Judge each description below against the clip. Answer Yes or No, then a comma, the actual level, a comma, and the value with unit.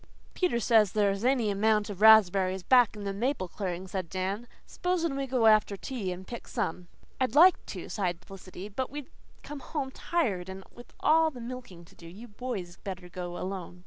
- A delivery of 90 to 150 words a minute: No, average, 195 wpm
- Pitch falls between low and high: No, high, 205 Hz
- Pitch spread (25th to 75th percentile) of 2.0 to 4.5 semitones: No, average, 5.3 semitones